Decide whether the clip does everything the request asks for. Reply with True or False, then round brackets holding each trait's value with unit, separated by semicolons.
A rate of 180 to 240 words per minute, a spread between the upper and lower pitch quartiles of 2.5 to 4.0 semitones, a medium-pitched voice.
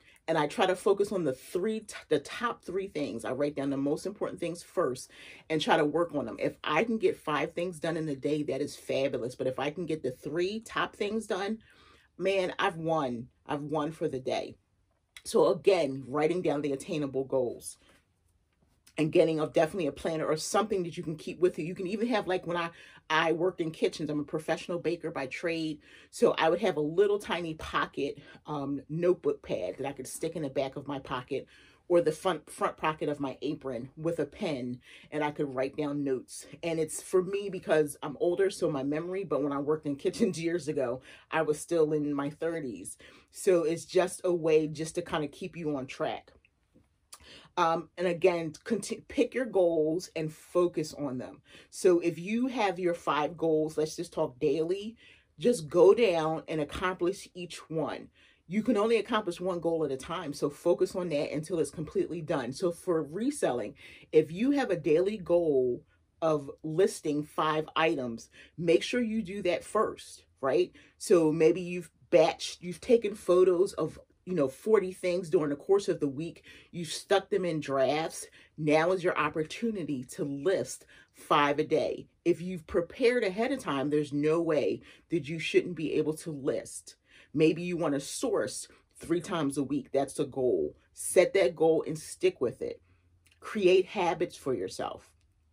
True (195 wpm; 3.6 semitones; 165 Hz)